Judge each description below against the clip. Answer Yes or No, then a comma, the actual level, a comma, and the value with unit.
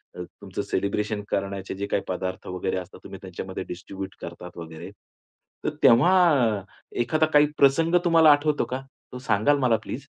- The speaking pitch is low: Yes, low, 105 Hz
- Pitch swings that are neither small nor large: No, wide, 7.4 semitones